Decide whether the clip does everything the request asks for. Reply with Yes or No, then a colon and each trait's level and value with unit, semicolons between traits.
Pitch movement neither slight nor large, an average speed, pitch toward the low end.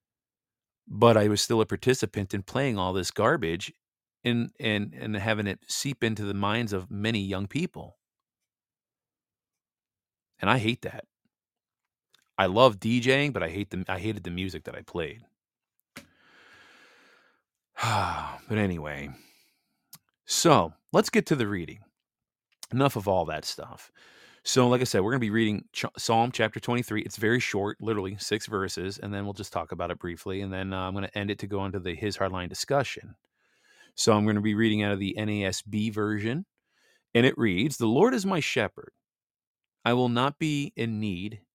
Yes: average, 3.3 semitones; average, 175 wpm; low, 105 Hz